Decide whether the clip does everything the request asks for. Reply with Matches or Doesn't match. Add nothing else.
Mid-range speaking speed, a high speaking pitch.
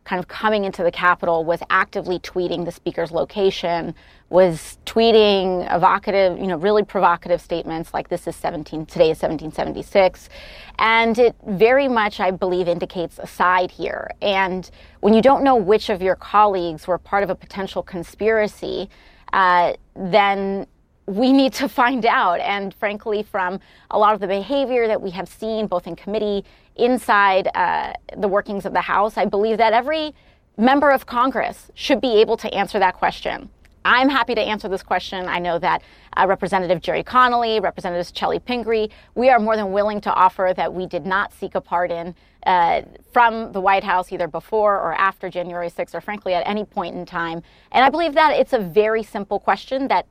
Matches